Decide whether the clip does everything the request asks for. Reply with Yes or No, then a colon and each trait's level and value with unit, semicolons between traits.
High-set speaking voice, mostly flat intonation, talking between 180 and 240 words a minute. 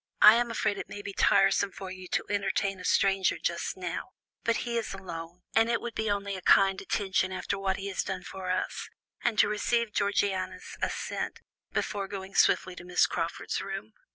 Yes: high, 195 Hz; narrow, 1.7 semitones; average, 195 wpm